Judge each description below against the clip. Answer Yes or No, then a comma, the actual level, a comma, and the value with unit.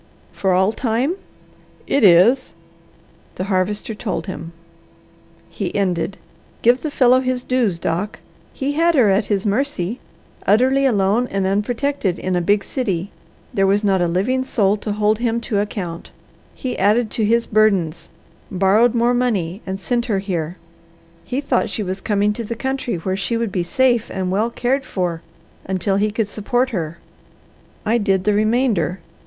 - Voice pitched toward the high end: Yes, high, 210 Hz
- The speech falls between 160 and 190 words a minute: Yes, average, 165 wpm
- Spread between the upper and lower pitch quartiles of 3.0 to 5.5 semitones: Yes, average, 4.1 semitones